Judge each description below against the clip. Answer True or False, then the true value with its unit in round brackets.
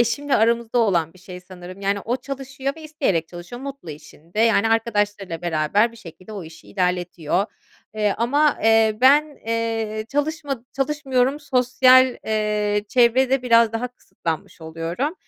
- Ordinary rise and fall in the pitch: False (5.7 semitones)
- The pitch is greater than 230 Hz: False (225 Hz)